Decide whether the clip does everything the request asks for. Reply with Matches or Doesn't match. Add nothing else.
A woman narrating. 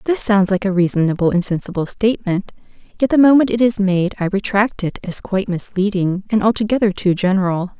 Matches